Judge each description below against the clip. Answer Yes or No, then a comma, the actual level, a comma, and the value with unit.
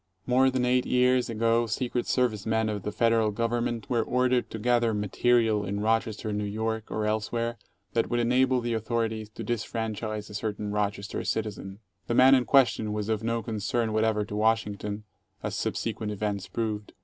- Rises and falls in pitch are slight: Yes, narrow, 2.1 semitones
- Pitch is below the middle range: Yes, low, 110 Hz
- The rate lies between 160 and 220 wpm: Yes, average, 175 wpm